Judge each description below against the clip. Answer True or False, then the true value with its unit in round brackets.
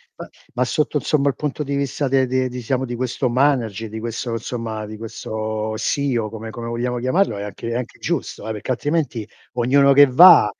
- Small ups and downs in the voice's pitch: False (3.5 semitones)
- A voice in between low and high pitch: False (125 Hz)